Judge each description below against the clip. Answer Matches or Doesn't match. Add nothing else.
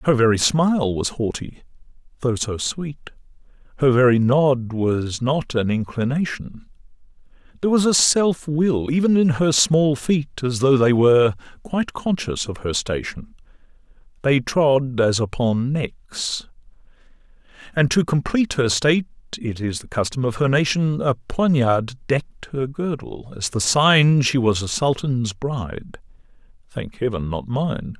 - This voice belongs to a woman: Doesn't match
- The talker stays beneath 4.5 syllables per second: Matches